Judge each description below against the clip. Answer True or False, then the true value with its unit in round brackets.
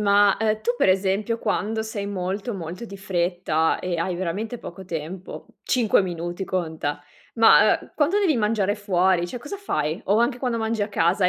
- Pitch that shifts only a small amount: False (4.0 semitones)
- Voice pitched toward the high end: True (200 Hz)